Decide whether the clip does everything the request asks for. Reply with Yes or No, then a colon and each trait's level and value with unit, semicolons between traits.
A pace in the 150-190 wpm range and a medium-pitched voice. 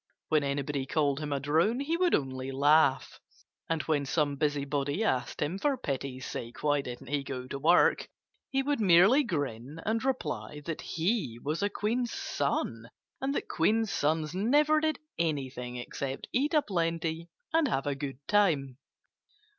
Yes: average, 160 wpm; medium, 150 Hz